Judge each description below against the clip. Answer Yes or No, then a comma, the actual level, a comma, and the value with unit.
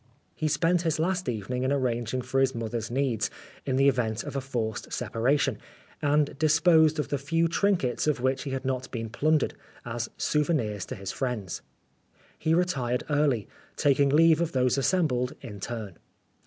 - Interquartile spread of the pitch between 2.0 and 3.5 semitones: No, average, 4.2 semitones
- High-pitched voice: No, low, 135 Hz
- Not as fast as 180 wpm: Yes, average, 170 wpm